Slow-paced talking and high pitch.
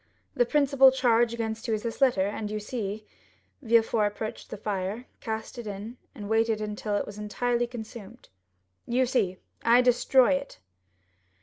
No: average, 160 wpm; high, 225 Hz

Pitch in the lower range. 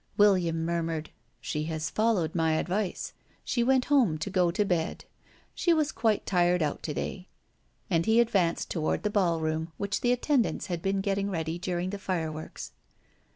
No: medium, 180 Hz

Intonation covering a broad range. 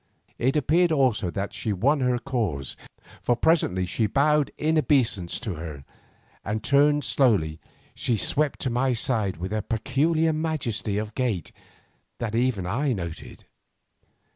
Yes: wide, 6.1 semitones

